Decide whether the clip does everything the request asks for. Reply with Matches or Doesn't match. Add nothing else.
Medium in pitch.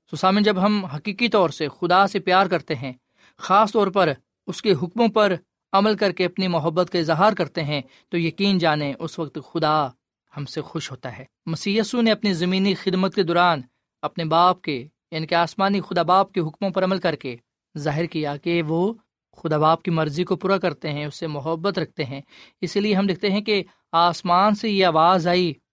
Matches